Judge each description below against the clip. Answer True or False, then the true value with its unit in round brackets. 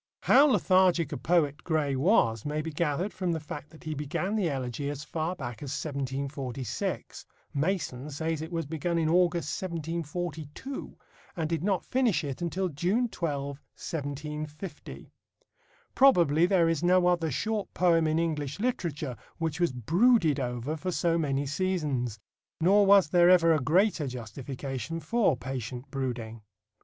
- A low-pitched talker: False (160 Hz)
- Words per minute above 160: False (150 wpm)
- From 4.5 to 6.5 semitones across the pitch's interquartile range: False (4.0 semitones)